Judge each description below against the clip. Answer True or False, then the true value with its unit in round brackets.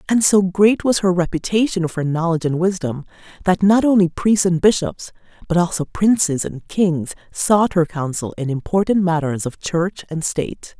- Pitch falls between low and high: True (175 Hz)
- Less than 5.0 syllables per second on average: True (4.8 syllables/s)